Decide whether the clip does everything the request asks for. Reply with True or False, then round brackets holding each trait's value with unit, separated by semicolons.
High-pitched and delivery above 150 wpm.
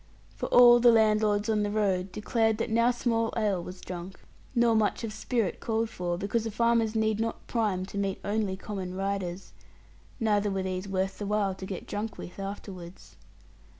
True (210 Hz; 185 wpm)